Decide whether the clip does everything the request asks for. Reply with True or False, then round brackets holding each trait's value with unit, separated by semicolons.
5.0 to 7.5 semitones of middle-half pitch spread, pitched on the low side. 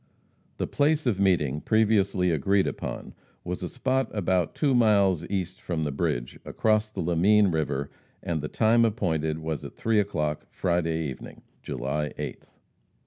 True (5.3 semitones; 90 Hz)